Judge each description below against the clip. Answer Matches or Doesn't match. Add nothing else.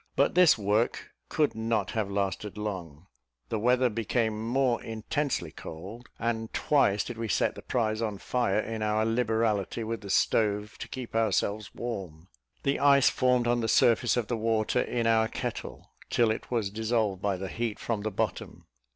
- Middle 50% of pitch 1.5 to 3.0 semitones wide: Matches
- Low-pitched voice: Matches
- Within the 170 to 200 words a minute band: Matches